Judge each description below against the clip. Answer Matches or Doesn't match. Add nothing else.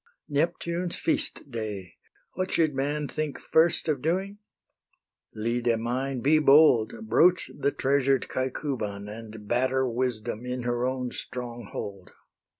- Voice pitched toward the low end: Matches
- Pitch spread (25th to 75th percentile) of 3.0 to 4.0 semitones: Doesn't match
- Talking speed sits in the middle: Doesn't match